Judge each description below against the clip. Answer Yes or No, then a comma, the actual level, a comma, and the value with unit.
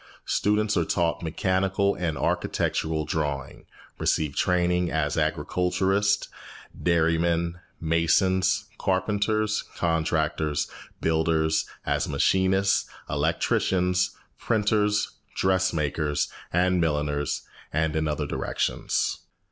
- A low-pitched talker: Yes, very low, 85 Hz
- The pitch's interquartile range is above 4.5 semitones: No, average, 3.1 semitones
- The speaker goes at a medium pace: No, slow, 85 wpm